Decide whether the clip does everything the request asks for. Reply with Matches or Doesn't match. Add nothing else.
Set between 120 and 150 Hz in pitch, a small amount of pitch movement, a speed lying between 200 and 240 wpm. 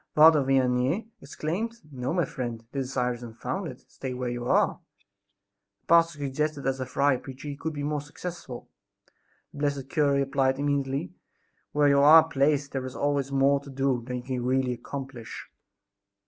Doesn't match